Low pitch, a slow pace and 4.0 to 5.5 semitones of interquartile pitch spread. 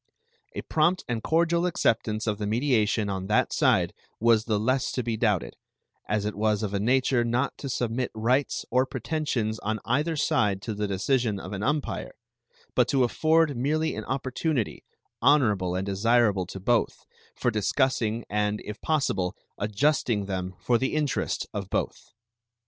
No: low, 115 Hz; average, 160 wpm; average, 4.3 semitones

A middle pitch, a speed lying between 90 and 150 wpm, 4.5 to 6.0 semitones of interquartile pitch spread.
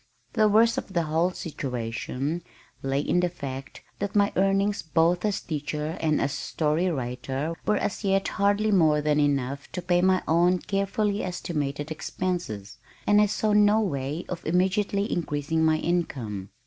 No: medium, 170 Hz; average, 160 wpm; average, 5.1 semitones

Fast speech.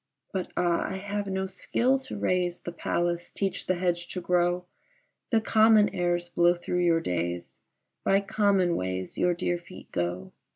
No: average, 165 wpm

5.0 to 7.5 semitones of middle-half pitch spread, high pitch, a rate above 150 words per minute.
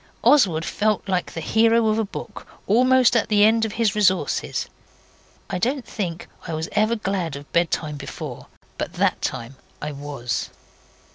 Yes: wide, 5.6 semitones; high, 200 Hz; average, 160 wpm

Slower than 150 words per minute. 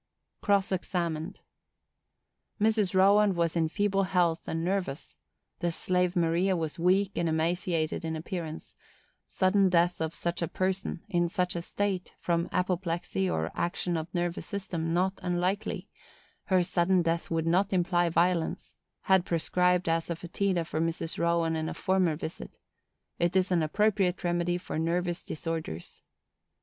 Yes: average, 140 wpm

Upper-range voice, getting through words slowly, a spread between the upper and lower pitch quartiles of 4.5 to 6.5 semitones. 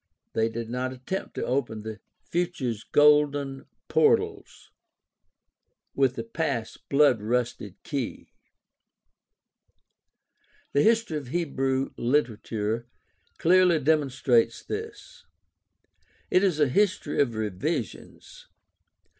No: low, 135 Hz; slow, 95 wpm; average, 5.2 semitones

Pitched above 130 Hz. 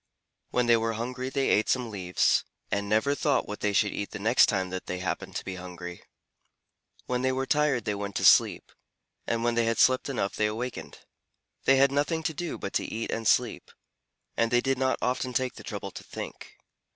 No: low, 120 Hz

